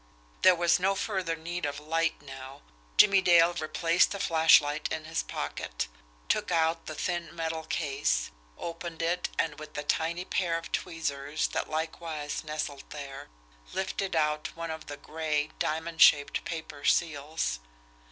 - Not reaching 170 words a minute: Yes, average, 150 wpm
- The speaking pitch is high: No, medium, 160 Hz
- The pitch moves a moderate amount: No, narrow, 2.2 semitones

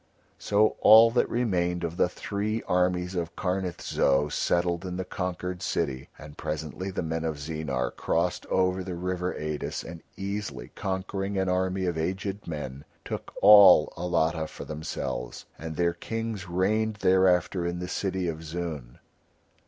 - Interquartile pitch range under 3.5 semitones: Yes, average, 2.8 semitones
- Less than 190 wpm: Yes, average, 150 wpm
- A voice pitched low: Yes, very low, 90 Hz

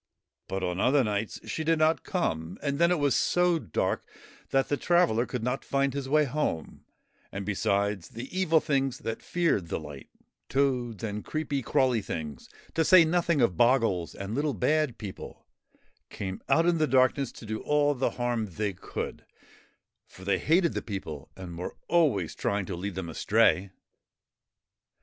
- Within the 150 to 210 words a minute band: Yes, average, 170 wpm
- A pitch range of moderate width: No, wide, 7.4 semitones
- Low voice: Yes, low, 125 Hz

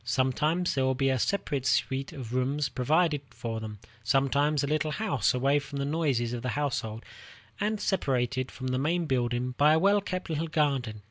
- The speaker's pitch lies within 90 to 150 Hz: Yes, medium, 140 Hz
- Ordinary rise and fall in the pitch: Yes, average, 3.4 semitones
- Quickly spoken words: No, average, 190 wpm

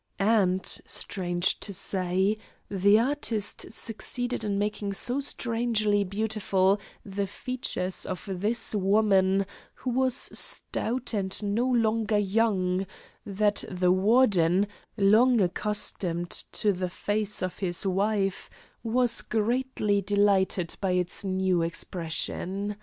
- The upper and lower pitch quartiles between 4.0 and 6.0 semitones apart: No, average, 2.7 semitones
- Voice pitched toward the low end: No, high, 205 Hz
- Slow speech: Yes, slow, 110 wpm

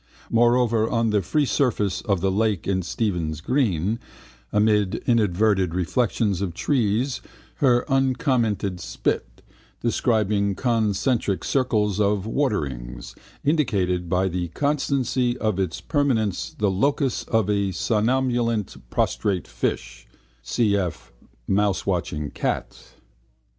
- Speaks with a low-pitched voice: Yes, low, 105 Hz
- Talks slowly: Yes, slow, 105 wpm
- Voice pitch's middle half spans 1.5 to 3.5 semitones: No, average, 4.6 semitones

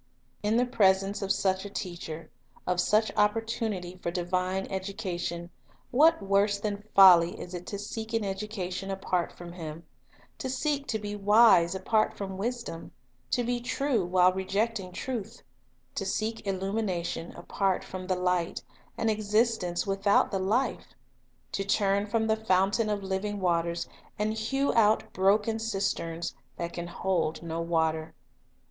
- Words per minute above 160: No, average, 150 wpm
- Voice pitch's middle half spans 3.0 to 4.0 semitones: Yes, average, 3.3 semitones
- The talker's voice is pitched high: Yes, high, 195 Hz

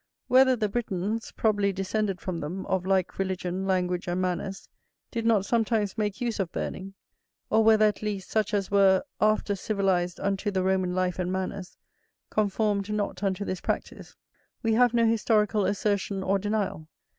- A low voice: No, high, 200 Hz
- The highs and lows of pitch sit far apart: No, narrow, 2.4 semitones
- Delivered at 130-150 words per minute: No, average, 165 wpm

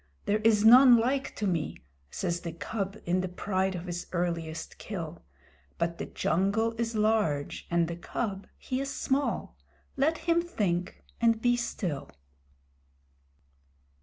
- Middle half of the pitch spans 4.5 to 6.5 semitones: Yes, average, 5.1 semitones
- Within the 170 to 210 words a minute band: No, average, 140 wpm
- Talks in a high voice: Yes, high, 195 Hz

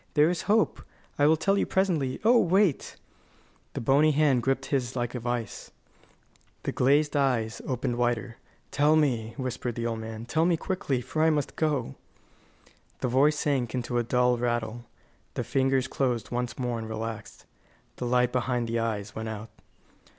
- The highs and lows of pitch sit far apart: No, average, 3.8 semitones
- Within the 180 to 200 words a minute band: No, average, 170 wpm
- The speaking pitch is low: Yes, low, 125 Hz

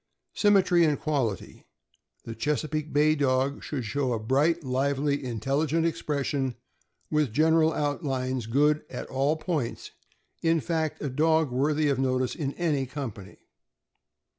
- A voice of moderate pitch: Yes, medium, 145 Hz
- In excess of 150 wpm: No, slow, 135 wpm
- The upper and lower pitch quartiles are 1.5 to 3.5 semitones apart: Yes, average, 3.0 semitones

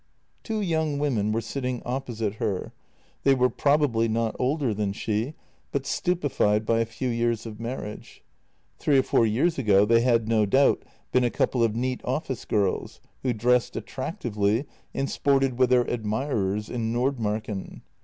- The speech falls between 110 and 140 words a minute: No, average, 160 wpm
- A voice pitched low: Yes, low, 120 Hz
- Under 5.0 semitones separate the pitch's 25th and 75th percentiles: Yes, average, 3.7 semitones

